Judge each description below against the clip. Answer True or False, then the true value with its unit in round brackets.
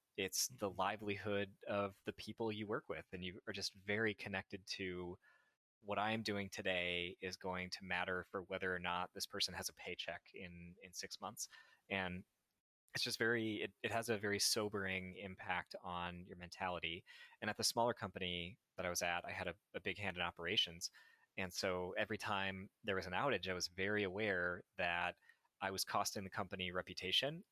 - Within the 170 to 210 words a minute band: True (190 wpm)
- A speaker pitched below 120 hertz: True (95 Hz)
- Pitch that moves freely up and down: False (2.4 semitones)